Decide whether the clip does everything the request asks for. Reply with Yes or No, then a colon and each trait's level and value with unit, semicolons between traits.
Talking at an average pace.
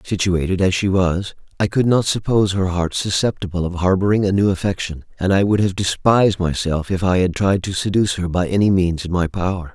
No: fast, 215 wpm